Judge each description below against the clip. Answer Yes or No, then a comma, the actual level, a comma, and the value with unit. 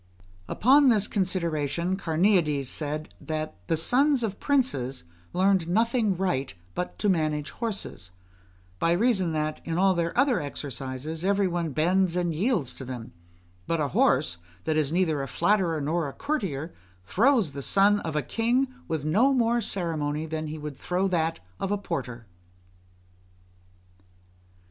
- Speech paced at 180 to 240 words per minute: No, average, 150 wpm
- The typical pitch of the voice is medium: Yes, medium, 170 Hz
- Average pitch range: Yes, average, 5.0 semitones